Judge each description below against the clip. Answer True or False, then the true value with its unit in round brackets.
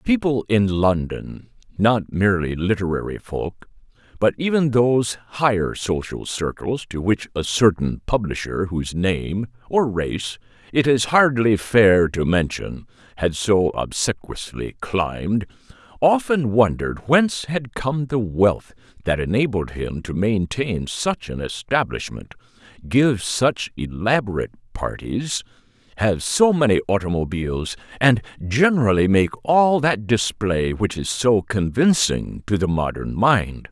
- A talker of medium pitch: False (110 Hz)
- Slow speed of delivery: True (115 wpm)